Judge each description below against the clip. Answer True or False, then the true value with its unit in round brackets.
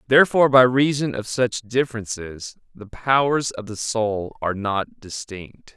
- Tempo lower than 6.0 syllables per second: True (4.5 syllables/s)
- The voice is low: True (115 Hz)